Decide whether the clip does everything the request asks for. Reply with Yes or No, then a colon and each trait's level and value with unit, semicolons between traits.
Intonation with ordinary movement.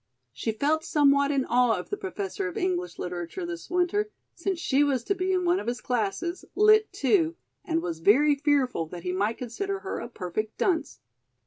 No: wide, 7.9 semitones